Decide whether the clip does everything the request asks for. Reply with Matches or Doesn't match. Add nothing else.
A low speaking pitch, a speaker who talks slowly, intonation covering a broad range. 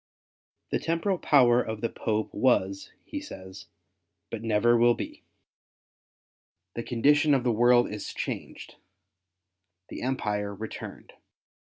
Doesn't match